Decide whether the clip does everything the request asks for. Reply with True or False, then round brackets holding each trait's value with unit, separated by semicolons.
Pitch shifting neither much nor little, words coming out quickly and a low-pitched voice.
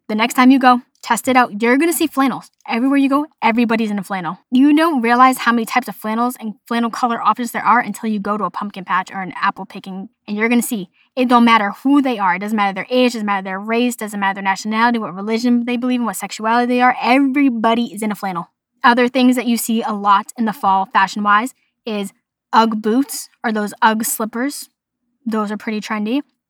False (3.2 semitones; 240 wpm; 230 Hz)